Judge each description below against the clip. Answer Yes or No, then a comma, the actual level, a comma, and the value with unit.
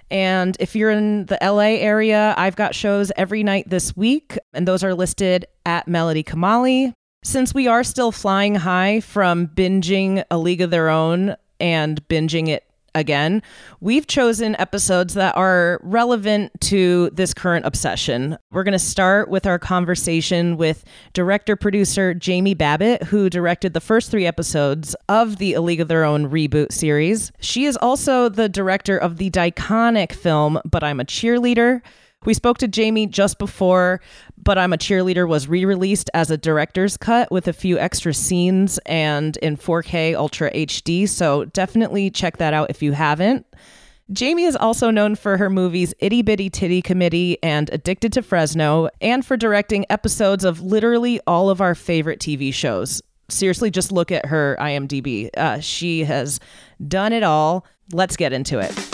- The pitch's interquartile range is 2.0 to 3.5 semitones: No, average, 4.2 semitones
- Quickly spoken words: No, average, 170 wpm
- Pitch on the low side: No, medium, 185 Hz